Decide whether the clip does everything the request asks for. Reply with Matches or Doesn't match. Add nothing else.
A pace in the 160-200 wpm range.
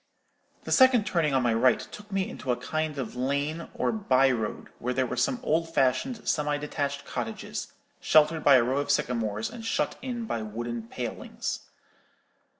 Matches